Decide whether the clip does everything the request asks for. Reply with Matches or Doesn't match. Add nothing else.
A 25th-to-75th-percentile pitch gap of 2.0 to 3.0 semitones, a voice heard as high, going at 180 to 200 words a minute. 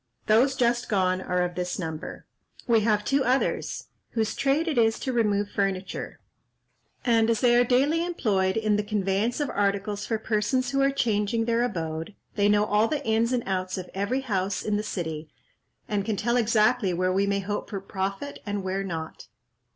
Doesn't match